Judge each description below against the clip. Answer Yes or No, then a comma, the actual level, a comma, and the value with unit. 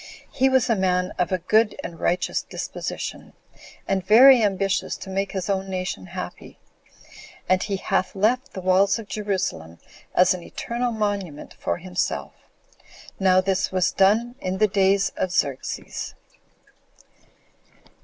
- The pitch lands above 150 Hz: Yes, high, 190 Hz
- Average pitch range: No, narrow, 2.3 semitones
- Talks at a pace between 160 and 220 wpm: No, average, 140 wpm